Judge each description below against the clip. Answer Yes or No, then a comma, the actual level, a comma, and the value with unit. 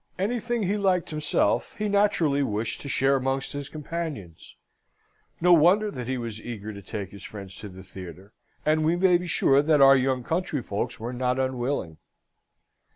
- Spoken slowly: No, average, 165 wpm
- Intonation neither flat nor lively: No, wide, 7.4 semitones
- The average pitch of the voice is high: No, low, 135 Hz